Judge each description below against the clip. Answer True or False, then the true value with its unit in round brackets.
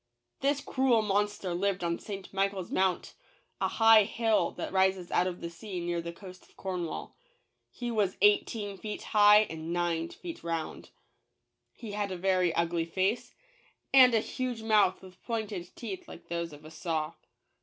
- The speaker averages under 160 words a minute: False (165 wpm)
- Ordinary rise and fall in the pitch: True (3.7 semitones)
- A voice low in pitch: False (190 Hz)